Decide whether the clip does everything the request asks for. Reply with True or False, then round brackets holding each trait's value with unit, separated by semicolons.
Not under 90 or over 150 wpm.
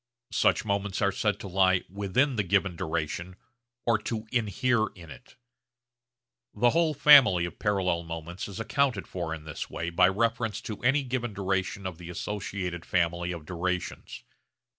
False (160 wpm)